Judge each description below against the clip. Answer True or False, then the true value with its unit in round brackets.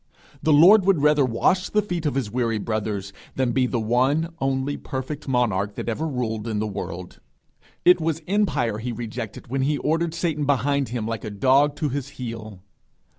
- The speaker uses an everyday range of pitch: True (4.9 semitones)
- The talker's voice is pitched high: False (130 Hz)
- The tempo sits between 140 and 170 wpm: False (185 wpm)